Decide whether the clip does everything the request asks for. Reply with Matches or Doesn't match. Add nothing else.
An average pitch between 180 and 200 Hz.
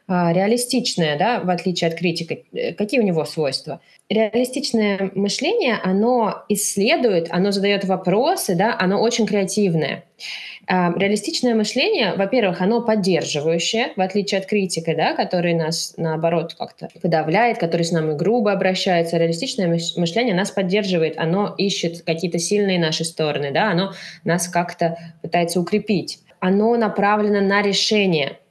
Matches